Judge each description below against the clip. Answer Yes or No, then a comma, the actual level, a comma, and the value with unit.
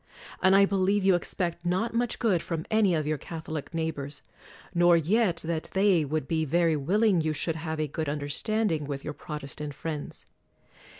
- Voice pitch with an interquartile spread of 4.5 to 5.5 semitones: No, average, 3.7 semitones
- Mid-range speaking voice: Yes, medium, 165 Hz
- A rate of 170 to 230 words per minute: Yes, average, 180 wpm